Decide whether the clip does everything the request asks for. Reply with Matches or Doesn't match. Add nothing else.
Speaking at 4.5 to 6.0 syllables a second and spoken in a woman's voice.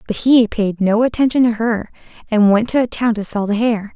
Matches